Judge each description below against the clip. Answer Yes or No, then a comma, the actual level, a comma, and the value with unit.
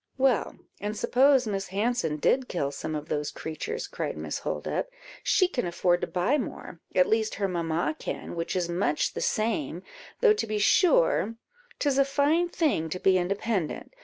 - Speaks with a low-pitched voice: No, high, 205 Hz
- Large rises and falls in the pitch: Yes, wide, 7.8 semitones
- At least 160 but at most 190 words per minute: Yes, average, 175 wpm